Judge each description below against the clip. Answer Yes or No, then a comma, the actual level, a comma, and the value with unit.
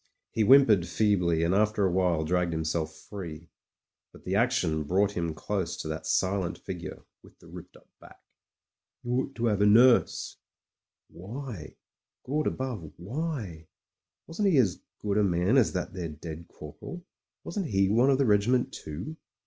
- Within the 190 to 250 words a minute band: No, average, 170 wpm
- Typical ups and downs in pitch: No, wide, 6.1 semitones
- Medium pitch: No, low, 100 Hz